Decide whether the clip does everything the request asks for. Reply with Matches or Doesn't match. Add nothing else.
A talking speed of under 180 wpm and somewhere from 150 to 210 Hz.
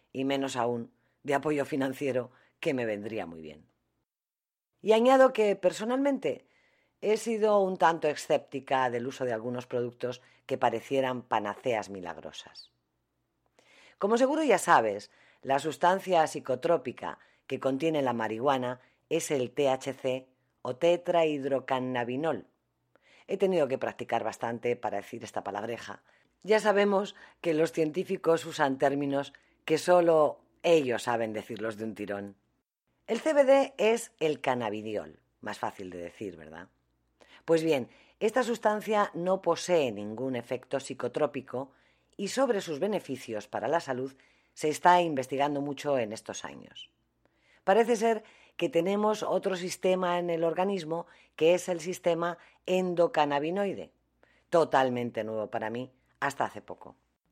Doesn't match